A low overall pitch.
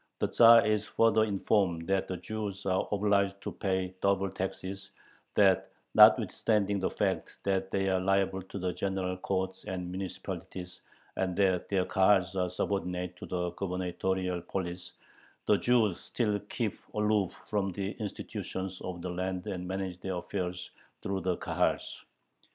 Yes: very low, 95 Hz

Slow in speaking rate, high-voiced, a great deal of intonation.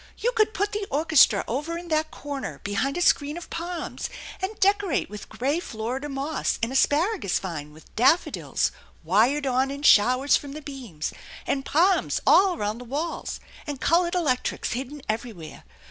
No: average, 165 wpm; very high, 285 Hz; wide, 5.8 semitones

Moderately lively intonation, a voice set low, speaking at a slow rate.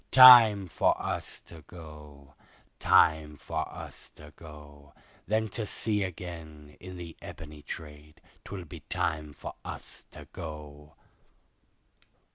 Yes: average, 3.4 semitones; very low, 80 Hz; slow, 120 wpm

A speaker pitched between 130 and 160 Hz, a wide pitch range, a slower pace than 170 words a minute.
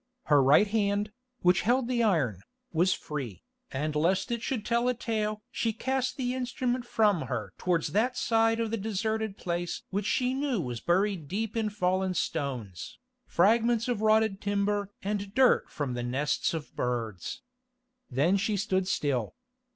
No: high, 200 Hz; wide, 6.2 semitones; average, 160 wpm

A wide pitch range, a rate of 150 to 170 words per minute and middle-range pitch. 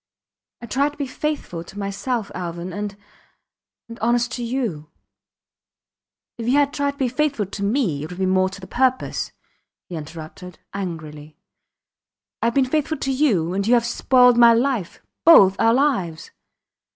No: wide, 6.2 semitones; average, 165 wpm; high, 230 Hz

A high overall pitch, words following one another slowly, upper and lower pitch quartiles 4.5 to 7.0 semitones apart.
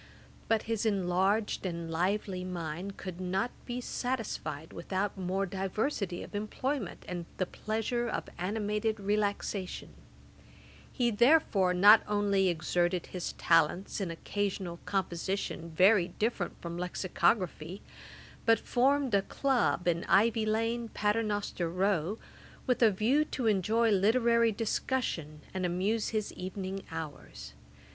No: high, 200 Hz; slow, 120 wpm; average, 3.7 semitones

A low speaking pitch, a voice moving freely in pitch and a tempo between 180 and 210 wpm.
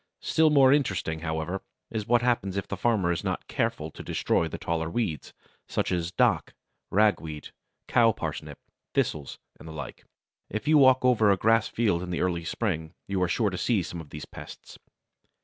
Yes: very low, 95 Hz; wide, 5.7 semitones; average, 185 wpm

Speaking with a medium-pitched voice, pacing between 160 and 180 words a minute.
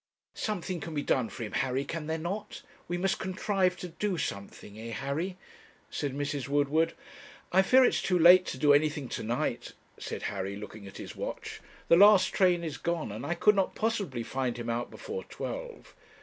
No: medium, 160 Hz; average, 195 wpm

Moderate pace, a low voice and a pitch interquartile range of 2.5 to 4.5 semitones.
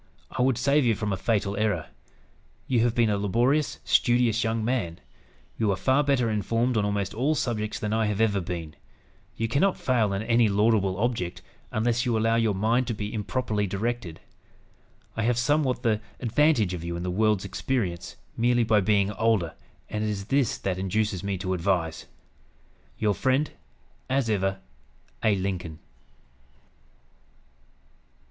Yes: average, 160 wpm; low, 110 Hz; average, 3.5 semitones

